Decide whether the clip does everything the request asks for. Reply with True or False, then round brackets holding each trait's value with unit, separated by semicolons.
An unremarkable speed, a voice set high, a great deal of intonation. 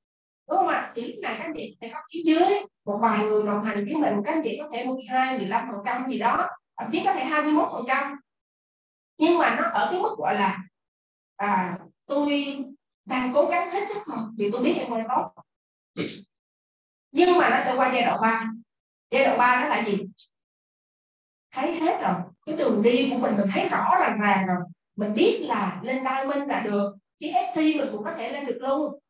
True (205 wpm; 255 Hz; 6.2 semitones)